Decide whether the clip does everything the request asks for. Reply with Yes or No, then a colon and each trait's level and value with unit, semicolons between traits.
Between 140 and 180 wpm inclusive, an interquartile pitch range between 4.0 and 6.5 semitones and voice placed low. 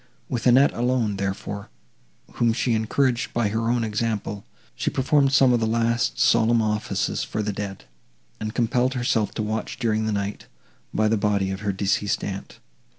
No: average, 170 wpm; narrow, 2.6 semitones; low, 110 Hz